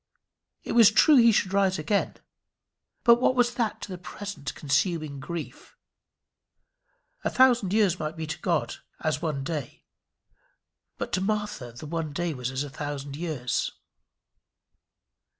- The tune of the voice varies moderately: No, wide, 6.0 semitones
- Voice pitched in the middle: Yes, medium, 170 Hz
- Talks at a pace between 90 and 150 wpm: Yes, average, 140 wpm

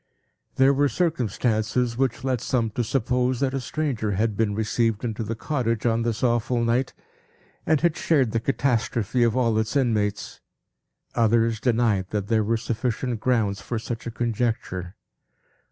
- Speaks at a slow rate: No, average, 155 wpm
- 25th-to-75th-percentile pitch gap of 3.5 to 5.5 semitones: No, narrow, 2.4 semitones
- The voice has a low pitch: Yes, low, 115 Hz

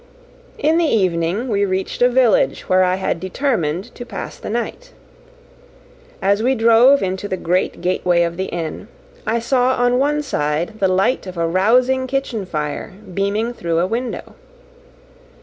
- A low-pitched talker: No, high, 200 Hz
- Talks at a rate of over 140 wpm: Yes, average, 160 wpm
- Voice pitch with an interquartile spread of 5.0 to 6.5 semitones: Yes, average, 5.3 semitones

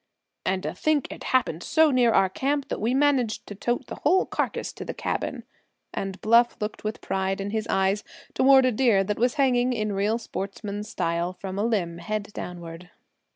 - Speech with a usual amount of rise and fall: Yes, average, 4.5 semitones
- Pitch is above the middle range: Yes, high, 215 Hz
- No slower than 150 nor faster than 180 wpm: No, average, 195 wpm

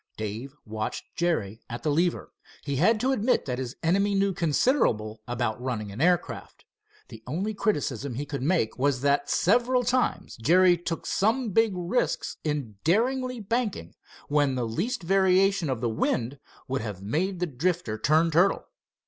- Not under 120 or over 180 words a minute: Yes, average, 160 wpm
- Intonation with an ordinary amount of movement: No, wide, 8.0 semitones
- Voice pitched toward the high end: No, medium, 160 Hz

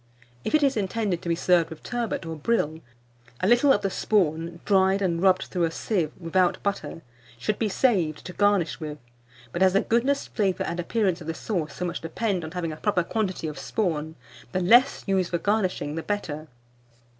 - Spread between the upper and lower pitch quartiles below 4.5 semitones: Yes, average, 4.0 semitones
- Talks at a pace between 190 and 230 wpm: Yes, average, 200 wpm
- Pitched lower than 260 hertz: Yes, medium, 185 Hz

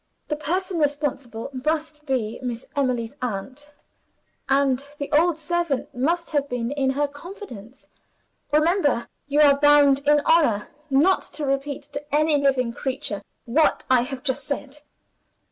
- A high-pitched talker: Yes, very high, 285 Hz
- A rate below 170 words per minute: Yes, average, 140 wpm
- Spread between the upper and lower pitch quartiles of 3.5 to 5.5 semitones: No, average, 2.8 semitones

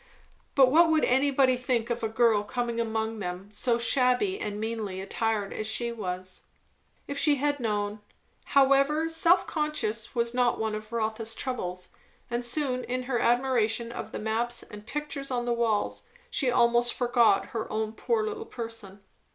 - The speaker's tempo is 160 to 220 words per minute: Yes, average, 170 wpm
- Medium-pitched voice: No, high, 235 Hz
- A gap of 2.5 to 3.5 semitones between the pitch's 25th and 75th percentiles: Yes, average, 3.2 semitones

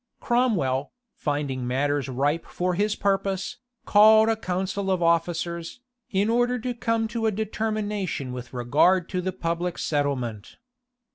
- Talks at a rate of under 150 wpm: Yes, slow, 135 wpm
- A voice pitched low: No, medium, 180 Hz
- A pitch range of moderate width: No, wide, 6.8 semitones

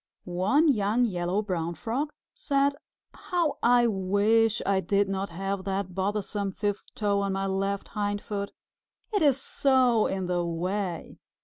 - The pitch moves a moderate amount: Yes, average, 3.4 semitones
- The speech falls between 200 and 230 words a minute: No, average, 140 wpm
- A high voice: Yes, high, 200 Hz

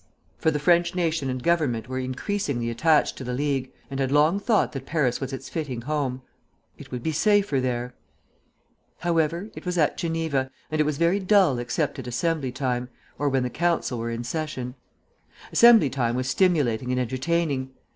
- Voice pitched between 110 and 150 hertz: Yes, medium, 140 Hz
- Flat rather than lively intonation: No, average, 4.7 semitones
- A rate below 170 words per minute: No, average, 180 wpm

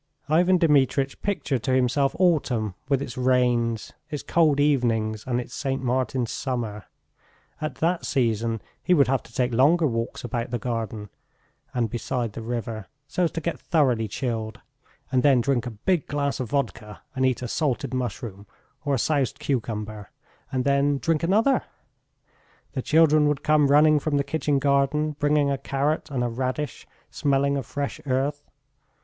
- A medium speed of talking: Yes, average, 165 wpm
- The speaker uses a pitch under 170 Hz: Yes, low, 135 Hz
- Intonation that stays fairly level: No, average, 3.7 semitones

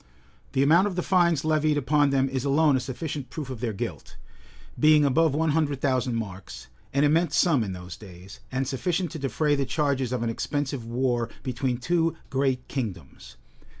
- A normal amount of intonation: Yes, average, 3.8 semitones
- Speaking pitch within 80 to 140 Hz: Yes, low, 135 Hz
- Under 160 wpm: No, average, 185 wpm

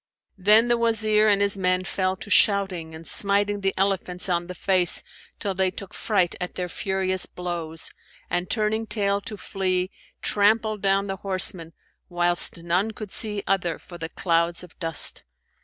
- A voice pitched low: No, high, 190 Hz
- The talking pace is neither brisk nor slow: Yes, average, 165 wpm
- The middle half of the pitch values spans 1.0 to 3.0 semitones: Yes, narrow, 2.4 semitones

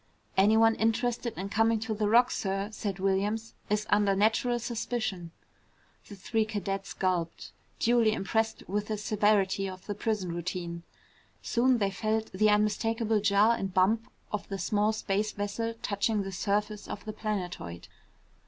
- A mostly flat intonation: Yes, narrow, 2.3 semitones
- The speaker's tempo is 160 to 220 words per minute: No, average, 150 wpm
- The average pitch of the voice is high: Yes, high, 210 Hz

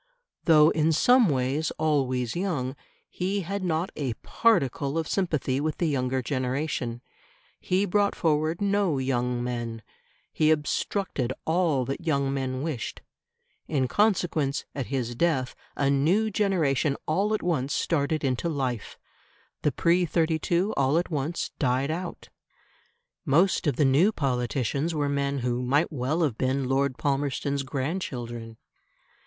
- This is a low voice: No, medium, 145 Hz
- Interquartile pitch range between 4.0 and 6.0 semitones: Yes, average, 4.4 semitones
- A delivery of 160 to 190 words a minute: No, slow, 135 wpm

